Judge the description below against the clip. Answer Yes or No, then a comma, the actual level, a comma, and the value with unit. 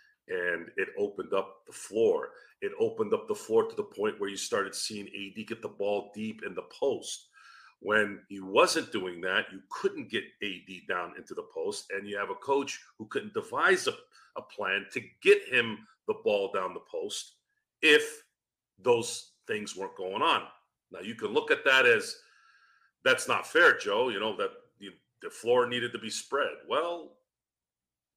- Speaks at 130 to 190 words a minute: Yes, average, 185 wpm